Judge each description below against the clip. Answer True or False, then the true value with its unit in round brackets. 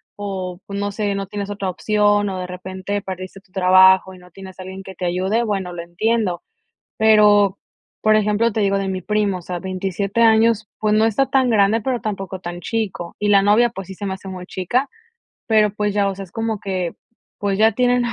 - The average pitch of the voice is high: True (200 Hz)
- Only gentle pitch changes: True (2.3 semitones)